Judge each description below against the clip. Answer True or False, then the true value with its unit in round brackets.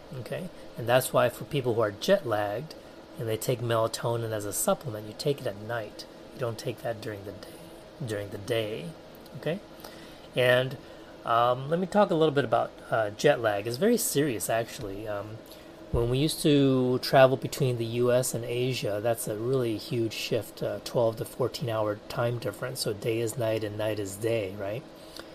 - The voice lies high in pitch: False (120 Hz)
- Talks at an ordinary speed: True (185 wpm)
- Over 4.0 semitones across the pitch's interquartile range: False (3.5 semitones)